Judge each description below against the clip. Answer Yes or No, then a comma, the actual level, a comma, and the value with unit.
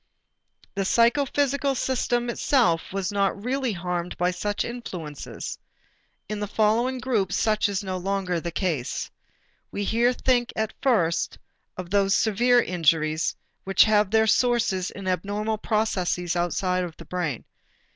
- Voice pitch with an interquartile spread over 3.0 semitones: Yes, average, 4.5 semitones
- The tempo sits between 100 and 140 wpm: Yes, slow, 135 wpm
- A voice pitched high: Yes, high, 200 Hz